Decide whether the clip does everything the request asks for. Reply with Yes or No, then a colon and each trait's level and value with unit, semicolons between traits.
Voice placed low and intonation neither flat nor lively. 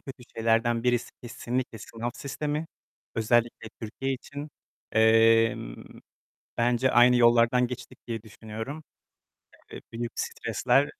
No: low, 120 Hz; narrow, 1.9 semitones